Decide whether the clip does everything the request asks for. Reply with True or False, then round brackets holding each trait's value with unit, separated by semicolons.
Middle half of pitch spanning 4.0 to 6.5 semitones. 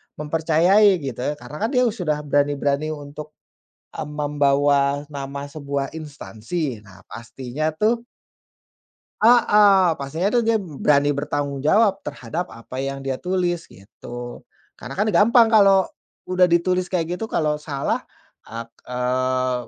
True (4.8 semitones)